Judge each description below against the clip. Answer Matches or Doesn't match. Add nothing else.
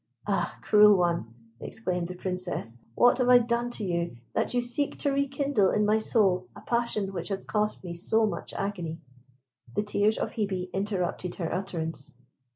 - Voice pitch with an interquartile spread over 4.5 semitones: Doesn't match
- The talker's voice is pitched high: Matches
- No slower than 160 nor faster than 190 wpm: Matches